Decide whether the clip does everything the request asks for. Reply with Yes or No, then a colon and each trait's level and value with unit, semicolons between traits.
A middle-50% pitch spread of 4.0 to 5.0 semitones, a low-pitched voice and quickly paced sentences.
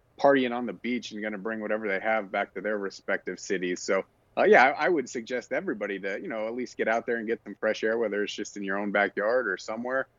No: narrow, 2.4 semitones; low, 110 Hz; fast, 270 wpm